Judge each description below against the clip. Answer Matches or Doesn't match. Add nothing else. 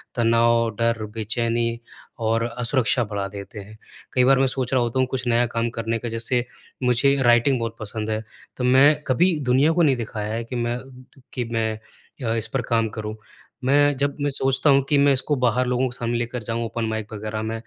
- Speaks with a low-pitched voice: Matches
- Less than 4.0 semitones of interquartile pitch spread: Matches